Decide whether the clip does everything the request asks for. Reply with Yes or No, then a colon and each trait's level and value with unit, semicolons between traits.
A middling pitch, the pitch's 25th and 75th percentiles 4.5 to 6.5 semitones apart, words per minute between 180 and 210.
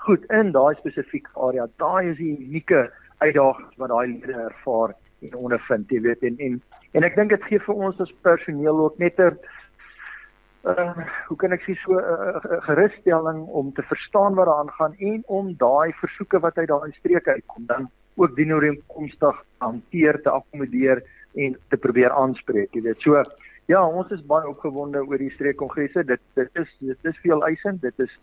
Yes: medium, 155 Hz; average, 5.0 semitones; average, 185 wpm